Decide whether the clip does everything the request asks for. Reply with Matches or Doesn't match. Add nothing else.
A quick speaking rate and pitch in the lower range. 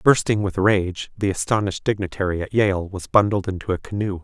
Doesn't match